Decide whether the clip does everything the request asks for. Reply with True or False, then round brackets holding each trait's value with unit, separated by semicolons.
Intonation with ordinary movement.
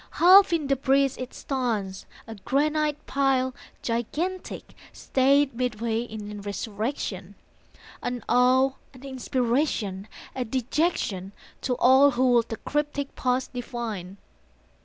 True (3.7 semitones)